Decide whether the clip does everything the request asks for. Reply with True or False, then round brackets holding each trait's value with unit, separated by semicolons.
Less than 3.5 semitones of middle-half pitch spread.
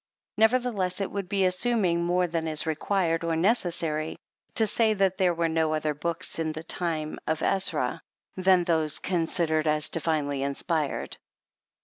True (3.1 semitones)